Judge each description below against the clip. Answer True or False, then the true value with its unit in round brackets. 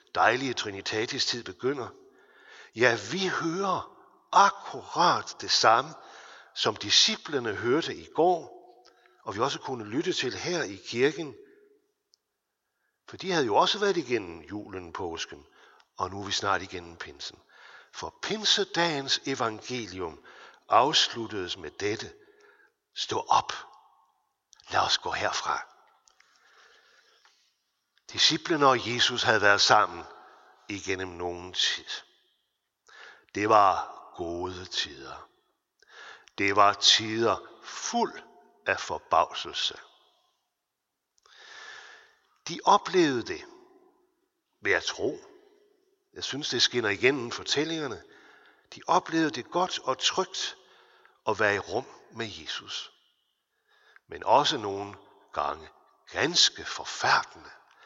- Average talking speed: False (105 wpm)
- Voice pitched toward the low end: False (360 Hz)